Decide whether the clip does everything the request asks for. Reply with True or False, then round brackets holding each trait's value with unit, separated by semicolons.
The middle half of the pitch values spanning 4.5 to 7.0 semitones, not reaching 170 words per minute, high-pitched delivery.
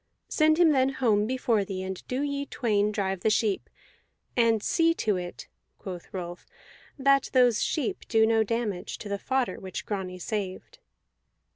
True (5.2 semitones; 160 wpm; 220 Hz)